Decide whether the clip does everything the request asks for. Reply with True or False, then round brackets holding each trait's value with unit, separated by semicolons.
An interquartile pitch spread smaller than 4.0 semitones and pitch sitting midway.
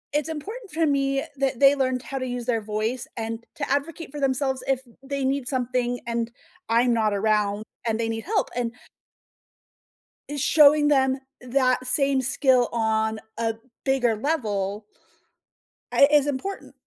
False (3.4 semitones; 255 Hz)